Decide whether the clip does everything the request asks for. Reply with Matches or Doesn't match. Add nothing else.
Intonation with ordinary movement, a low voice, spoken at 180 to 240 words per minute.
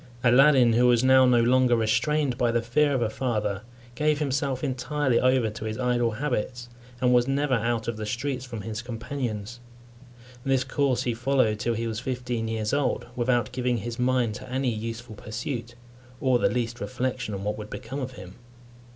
Doesn't match